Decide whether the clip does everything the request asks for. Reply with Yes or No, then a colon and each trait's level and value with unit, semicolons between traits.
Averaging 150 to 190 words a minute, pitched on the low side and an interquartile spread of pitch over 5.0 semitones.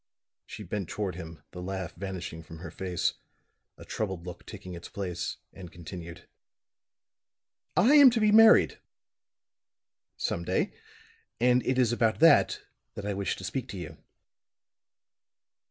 No: average, 140 wpm; very low, 95 Hz; wide, 5.5 semitones